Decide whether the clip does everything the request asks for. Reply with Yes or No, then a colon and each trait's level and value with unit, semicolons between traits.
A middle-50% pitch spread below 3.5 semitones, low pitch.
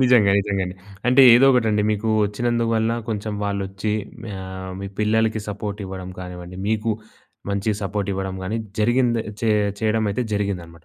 Yes: narrow, 2.6 semitones; low, 105 Hz